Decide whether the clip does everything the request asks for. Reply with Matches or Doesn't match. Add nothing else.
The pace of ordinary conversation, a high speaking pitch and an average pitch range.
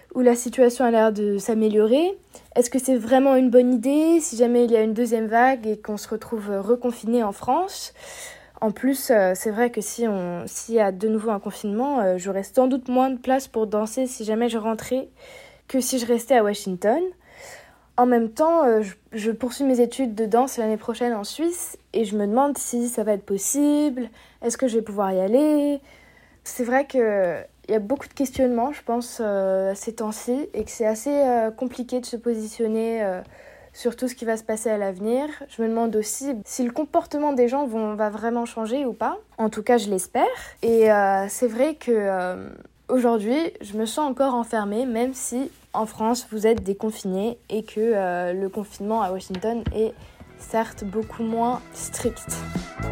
Matches